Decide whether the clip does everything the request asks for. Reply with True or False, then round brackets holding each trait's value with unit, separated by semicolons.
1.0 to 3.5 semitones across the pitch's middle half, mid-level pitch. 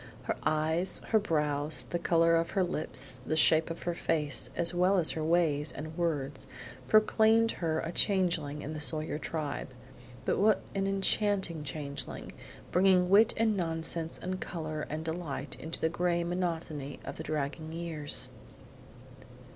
True (2.8 semitones; 165 Hz)